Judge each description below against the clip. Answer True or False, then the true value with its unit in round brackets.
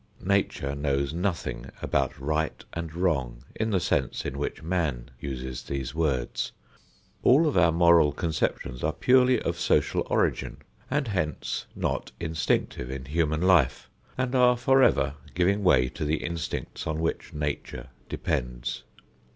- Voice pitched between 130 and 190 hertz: False (80 Hz)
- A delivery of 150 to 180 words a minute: False (140 wpm)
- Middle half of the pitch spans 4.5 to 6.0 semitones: True (5.2 semitones)